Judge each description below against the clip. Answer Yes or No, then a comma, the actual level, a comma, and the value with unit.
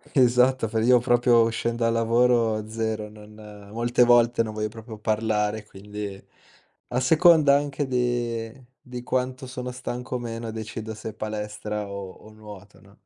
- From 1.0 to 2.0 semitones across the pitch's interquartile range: No, narrow, 2.4 semitones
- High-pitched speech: No, low, 115 Hz